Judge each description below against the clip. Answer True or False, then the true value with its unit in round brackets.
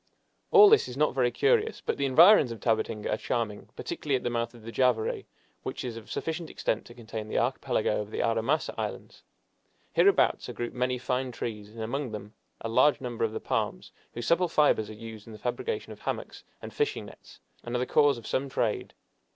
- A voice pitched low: True (120 Hz)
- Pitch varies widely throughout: False (3.9 semitones)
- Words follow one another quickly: True (210 wpm)